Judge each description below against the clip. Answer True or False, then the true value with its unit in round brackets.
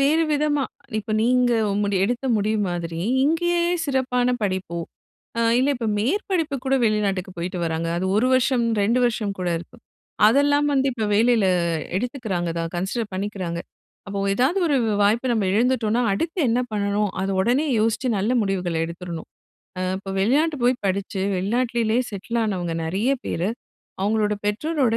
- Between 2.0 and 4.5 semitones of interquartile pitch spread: False (4.9 semitones)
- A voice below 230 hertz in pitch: True (220 Hz)